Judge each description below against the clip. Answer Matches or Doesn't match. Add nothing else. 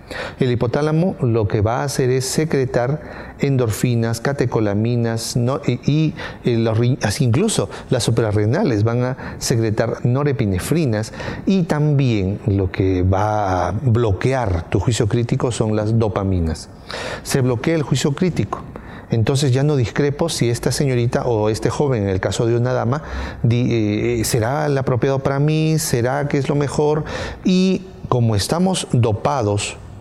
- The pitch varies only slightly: Doesn't match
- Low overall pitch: Matches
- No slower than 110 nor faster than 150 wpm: Matches